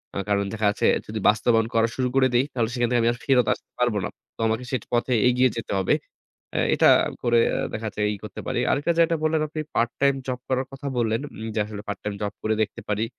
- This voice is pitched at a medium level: No, low, 120 Hz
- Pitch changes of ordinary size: Yes, average, 3.0 semitones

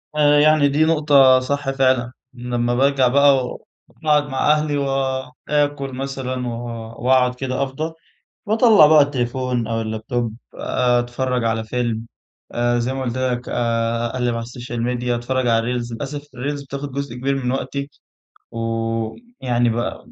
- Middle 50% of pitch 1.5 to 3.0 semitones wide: Yes, average, 2.7 semitones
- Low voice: Yes, low, 130 Hz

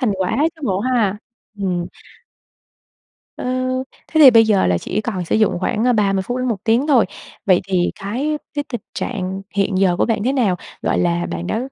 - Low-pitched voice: No, high, 205 Hz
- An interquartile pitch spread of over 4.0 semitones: Yes, average, 4.6 semitones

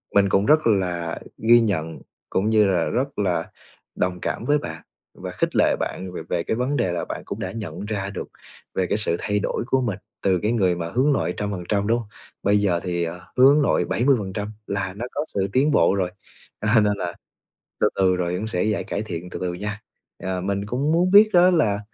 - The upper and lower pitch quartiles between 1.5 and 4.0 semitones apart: No, average, 4.5 semitones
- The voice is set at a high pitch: No, low, 100 Hz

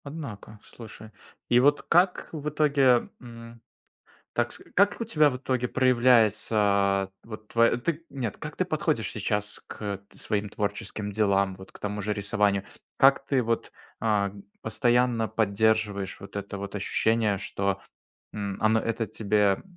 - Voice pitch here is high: No, low, 110 Hz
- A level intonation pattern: No, average, 3.6 semitones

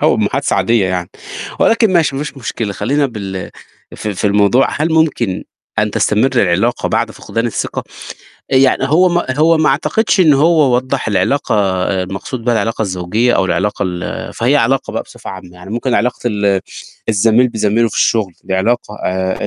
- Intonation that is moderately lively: No, wide, 5.7 semitones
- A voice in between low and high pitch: No, low, 115 Hz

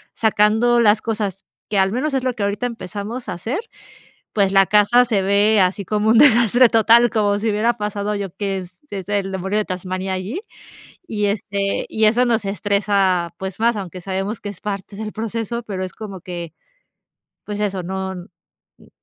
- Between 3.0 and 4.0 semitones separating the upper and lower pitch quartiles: No, narrow, 2.6 semitones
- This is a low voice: No, high, 205 Hz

